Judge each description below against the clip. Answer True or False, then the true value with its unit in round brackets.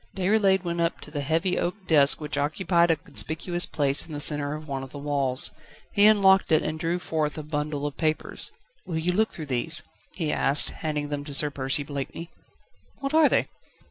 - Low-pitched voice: False (155 Hz)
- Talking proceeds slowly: False (205 wpm)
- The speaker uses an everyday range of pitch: True (3.3 semitones)